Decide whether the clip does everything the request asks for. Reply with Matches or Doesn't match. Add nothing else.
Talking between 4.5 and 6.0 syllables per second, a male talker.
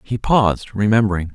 Matches